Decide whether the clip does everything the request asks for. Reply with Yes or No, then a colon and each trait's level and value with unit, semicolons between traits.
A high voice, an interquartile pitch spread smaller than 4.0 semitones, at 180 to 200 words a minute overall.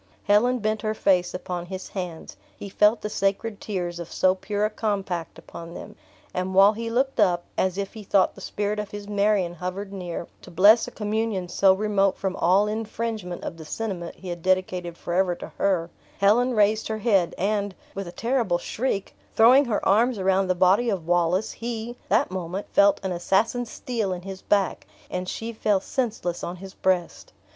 Yes: high, 195 Hz; average, 2.9 semitones; average, 190 wpm